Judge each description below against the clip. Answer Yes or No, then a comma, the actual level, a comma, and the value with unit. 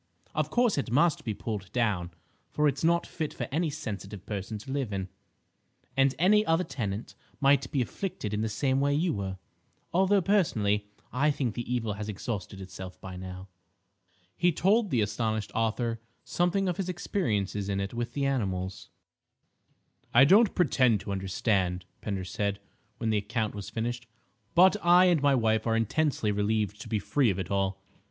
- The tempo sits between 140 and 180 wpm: Yes, average, 175 wpm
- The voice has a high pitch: No, low, 115 Hz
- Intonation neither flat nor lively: No, wide, 6.5 semitones